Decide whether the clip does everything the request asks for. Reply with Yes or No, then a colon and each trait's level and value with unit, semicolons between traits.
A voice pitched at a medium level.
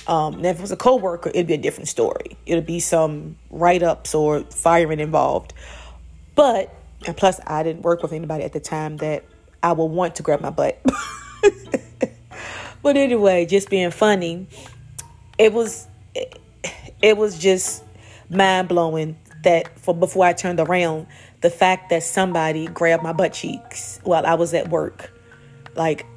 Yes: medium, 170 Hz